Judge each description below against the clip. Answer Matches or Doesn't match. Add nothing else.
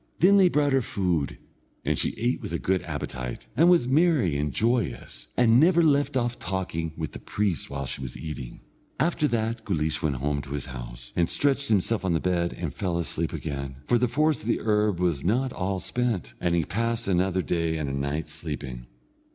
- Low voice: Matches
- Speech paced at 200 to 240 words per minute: Matches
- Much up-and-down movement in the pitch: Matches